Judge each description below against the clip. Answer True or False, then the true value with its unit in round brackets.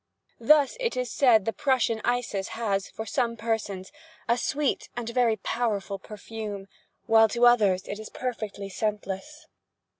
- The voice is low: False (225 Hz)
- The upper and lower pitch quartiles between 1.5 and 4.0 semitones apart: True (3.2 semitones)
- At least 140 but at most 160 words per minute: True (145 wpm)